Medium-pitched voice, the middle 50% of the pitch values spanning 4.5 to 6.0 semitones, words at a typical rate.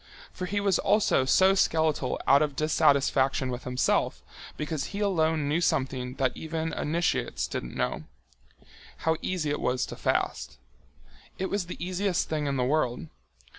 Yes: medium, 155 Hz; average, 4.8 semitones; average, 150 wpm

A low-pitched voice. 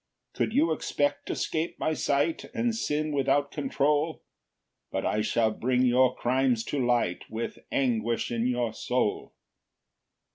Yes: low, 130 Hz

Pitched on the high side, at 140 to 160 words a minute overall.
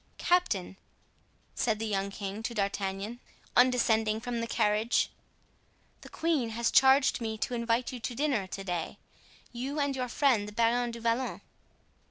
Yes: high, 230 Hz; average, 155 wpm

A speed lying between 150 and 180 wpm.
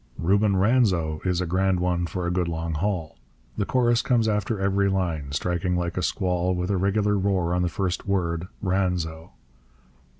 Yes: average, 175 wpm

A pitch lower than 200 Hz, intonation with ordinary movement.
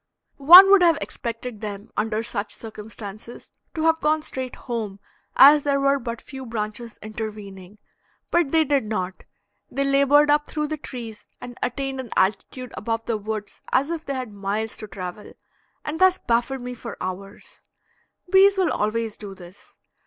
No: high, 235 Hz; average, 5.0 semitones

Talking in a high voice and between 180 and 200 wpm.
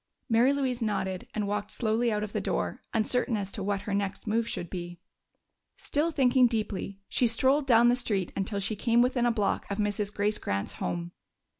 Yes: high, 215 Hz; average, 195 wpm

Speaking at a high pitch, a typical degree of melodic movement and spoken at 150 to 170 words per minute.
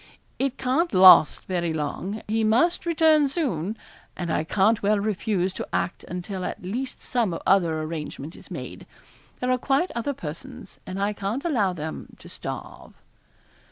No: high, 205 Hz; wide, 6.2 semitones; average, 160 wpm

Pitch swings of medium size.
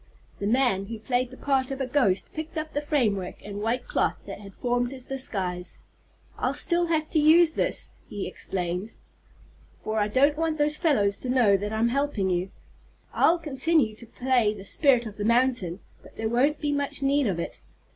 No: wide, 5.8 semitones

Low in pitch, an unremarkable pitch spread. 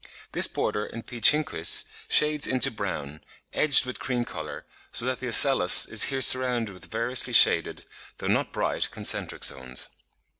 Yes: low, 120 Hz; average, 4.4 semitones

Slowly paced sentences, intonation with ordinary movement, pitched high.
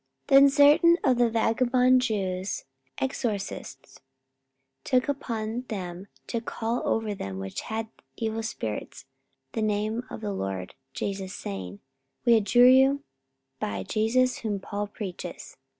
Yes: slow, 130 wpm; average, 4.3 semitones; high, 220 Hz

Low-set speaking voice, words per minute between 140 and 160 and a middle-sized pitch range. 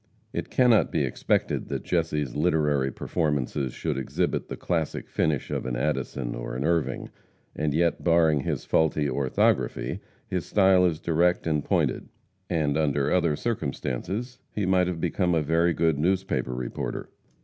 Yes: very low, 80 Hz; average, 150 wpm; average, 3.7 semitones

